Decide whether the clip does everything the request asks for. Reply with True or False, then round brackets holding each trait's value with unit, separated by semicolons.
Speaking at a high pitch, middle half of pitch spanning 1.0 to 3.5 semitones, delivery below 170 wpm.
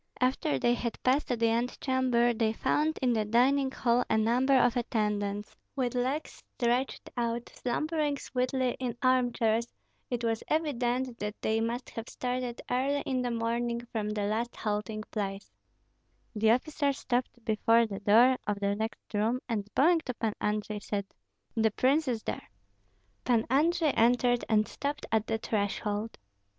True (235 Hz; 2.7 semitones; 160 wpm)